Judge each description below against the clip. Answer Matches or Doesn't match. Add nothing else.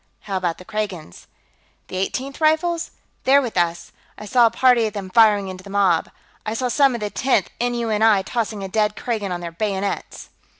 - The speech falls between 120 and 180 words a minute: Doesn't match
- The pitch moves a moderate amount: Matches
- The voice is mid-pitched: Doesn't match